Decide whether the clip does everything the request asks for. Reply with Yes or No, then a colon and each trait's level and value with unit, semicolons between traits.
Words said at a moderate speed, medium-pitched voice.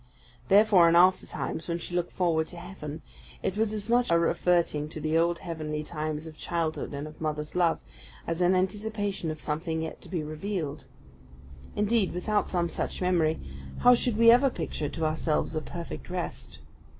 Yes: average, 175 wpm; medium, 170 Hz